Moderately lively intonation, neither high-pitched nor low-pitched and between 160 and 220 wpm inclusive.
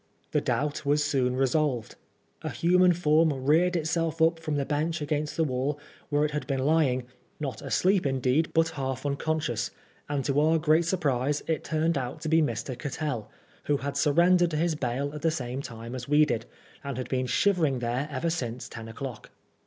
Yes: average, 3.6 semitones; medium, 145 Hz; average, 190 wpm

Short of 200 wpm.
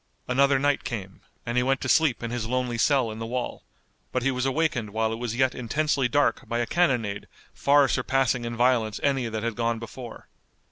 No: fast, 205 wpm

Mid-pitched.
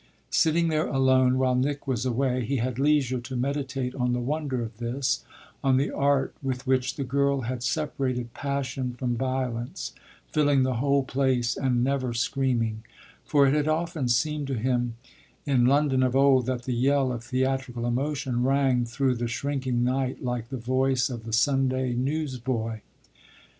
No: low, 130 Hz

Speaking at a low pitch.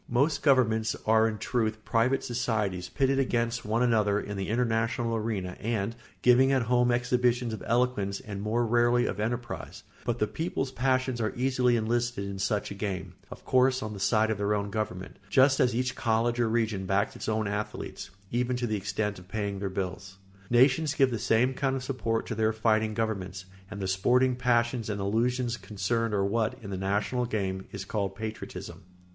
Yes: low, 115 Hz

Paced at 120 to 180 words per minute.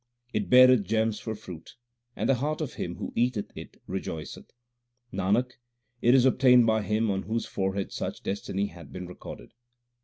Yes: average, 165 wpm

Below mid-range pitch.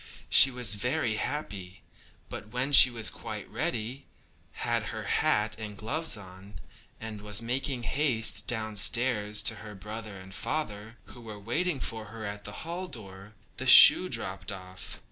Yes: low, 110 Hz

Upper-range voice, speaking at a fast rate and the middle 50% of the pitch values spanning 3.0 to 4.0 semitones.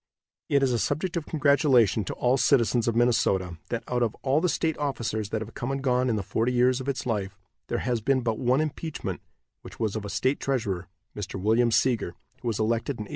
No: low, 120 Hz; fast, 230 wpm; average, 3.7 semitones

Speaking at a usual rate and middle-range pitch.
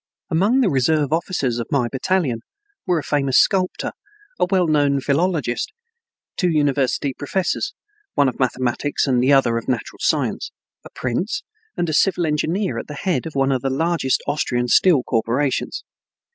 Yes: average, 160 wpm; medium, 145 Hz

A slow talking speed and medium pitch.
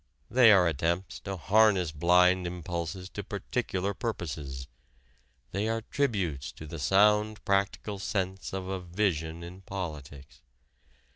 No: slow, 125 wpm; very low, 95 Hz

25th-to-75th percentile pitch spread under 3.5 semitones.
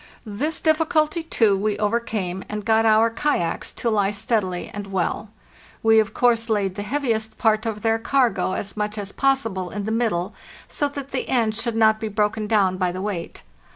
Yes: narrow, 2.4 semitones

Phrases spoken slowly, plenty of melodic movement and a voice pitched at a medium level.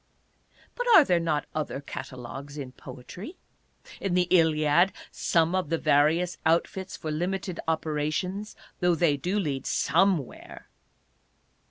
No: slow, 120 wpm; average, 3.8 semitones; medium, 165 Hz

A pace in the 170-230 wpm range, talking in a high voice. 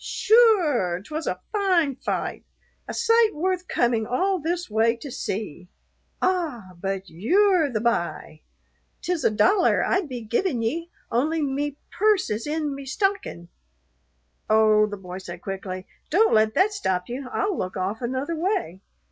No: average, 155 wpm; very high, 265 Hz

